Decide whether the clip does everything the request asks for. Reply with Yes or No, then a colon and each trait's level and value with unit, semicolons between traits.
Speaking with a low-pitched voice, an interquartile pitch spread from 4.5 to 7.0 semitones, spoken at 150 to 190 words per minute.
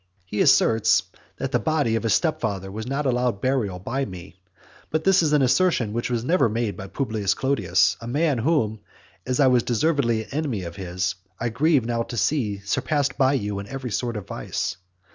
No: low, 120 Hz; average, 4.9 semitones; average, 200 wpm